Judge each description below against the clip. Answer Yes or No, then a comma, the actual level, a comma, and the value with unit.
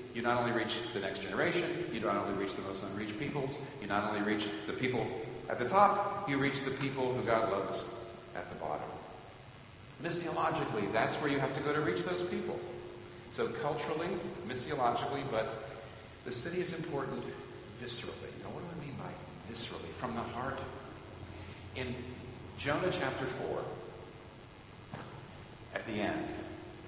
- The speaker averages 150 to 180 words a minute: Yes, average, 160 wpm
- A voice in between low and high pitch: No, low, 125 Hz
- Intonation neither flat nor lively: Yes, average, 4.2 semitones